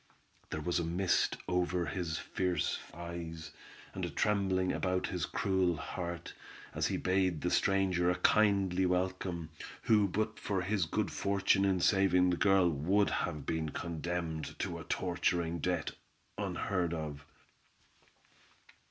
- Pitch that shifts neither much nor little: No, narrow, 2.2 semitones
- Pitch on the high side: No, very low, 90 Hz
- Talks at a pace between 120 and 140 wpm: Yes, slow, 135 wpm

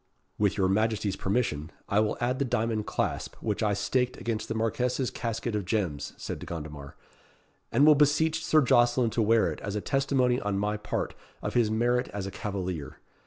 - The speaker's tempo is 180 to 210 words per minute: Yes, average, 190 wpm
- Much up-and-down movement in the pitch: No, average, 3.7 semitones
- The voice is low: Yes, low, 110 Hz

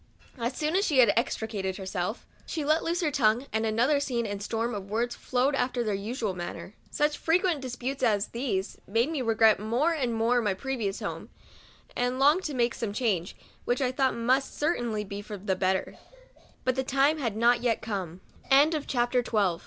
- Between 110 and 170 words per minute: Yes, average, 155 wpm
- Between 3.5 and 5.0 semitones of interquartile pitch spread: Yes, average, 4.2 semitones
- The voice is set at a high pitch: Yes, high, 240 Hz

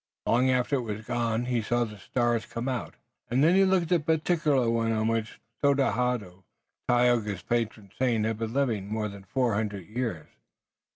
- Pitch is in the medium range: No, low, 120 Hz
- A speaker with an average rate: Yes, average, 180 wpm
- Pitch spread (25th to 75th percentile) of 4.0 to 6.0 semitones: No, average, 2.9 semitones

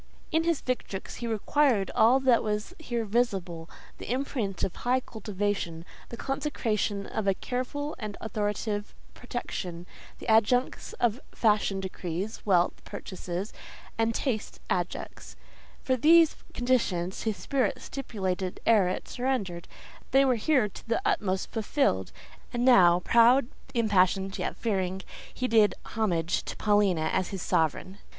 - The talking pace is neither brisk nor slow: No, slow, 130 wpm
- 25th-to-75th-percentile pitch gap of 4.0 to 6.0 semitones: Yes, average, 4.6 semitones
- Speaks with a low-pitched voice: No, high, 215 Hz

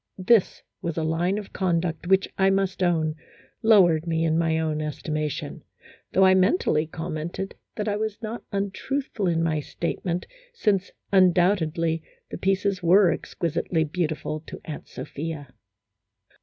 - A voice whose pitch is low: No, medium, 175 Hz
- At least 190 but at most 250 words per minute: No, average, 150 wpm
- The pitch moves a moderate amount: Yes, average, 3.3 semitones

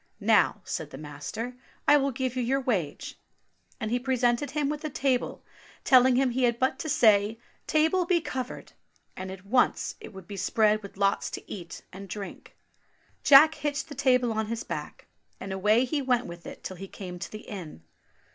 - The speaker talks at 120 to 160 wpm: No, average, 195 wpm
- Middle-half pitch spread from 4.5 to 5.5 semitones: Yes, average, 5.1 semitones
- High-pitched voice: Yes, high, 240 Hz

